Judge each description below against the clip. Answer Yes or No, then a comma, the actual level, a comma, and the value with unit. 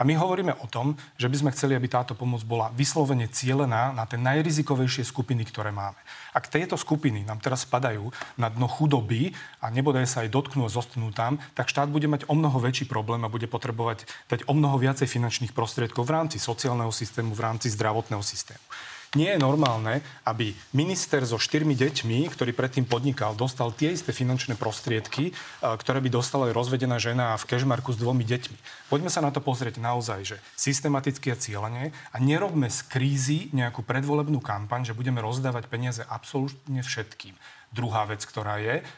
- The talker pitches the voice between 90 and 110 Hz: No, low, 125 Hz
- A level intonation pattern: No, average, 3.3 semitones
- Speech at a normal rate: No, fast, 180 wpm